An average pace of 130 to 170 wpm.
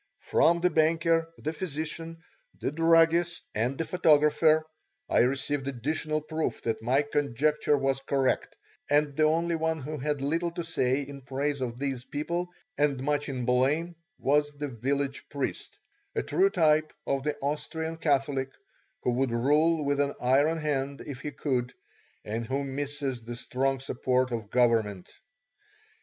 Yes: average, 150 wpm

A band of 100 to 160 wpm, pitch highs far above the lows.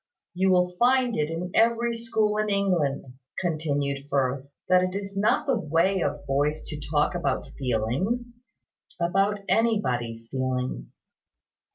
Yes: slow, 135 wpm; wide, 6.7 semitones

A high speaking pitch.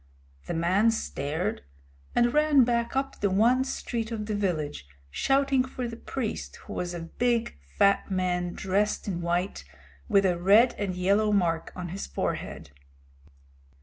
Yes: high, 200 Hz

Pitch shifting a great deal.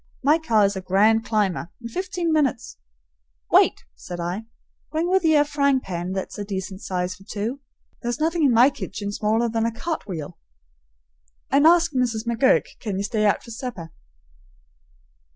Yes: wide, 6.5 semitones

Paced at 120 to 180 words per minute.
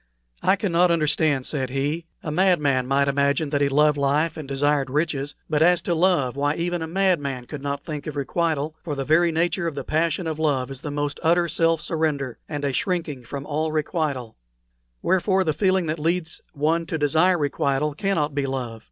No: average, 195 wpm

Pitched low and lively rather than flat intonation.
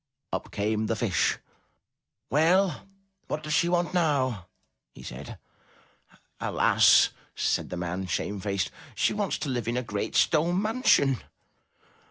Yes: low, 130 Hz; wide, 9.0 semitones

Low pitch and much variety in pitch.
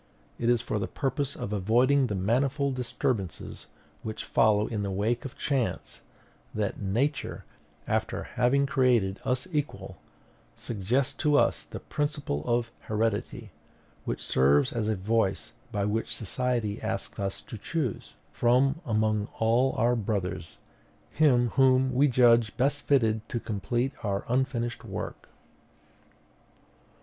No: low, 115 Hz; average, 3.8 semitones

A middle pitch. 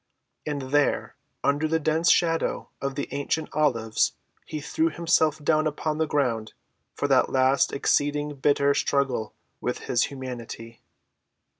Yes: medium, 145 Hz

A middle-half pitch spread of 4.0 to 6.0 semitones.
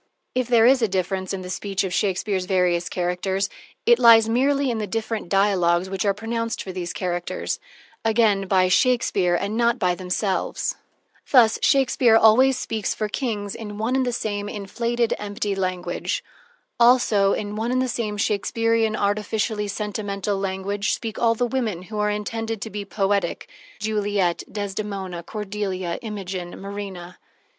No: average, 2.9 semitones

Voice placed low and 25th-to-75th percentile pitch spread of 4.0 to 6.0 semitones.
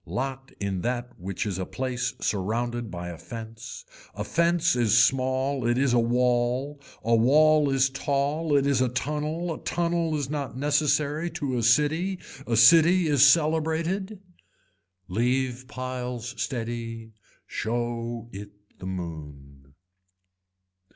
Yes: low, 130 Hz; average, 4.4 semitones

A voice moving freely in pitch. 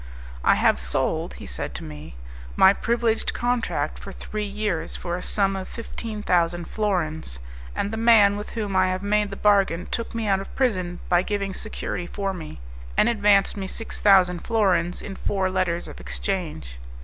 No: average, 3.3 semitones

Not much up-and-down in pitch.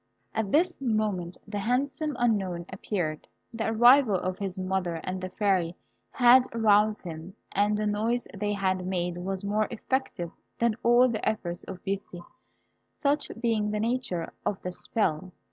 No: average, 3.9 semitones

